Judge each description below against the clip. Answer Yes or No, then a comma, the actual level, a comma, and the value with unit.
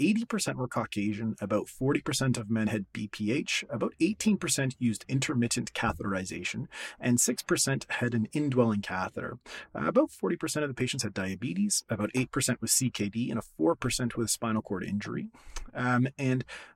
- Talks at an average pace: Yes, average, 145 wpm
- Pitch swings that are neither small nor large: Yes, average, 3.9 semitones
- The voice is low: Yes, low, 125 Hz